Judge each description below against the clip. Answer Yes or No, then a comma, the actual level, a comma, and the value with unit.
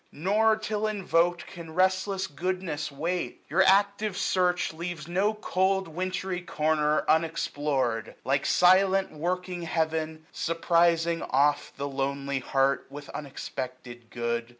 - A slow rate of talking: Yes, slow, 120 wpm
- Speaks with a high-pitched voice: No, medium, 165 Hz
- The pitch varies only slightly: No, average, 4.5 semitones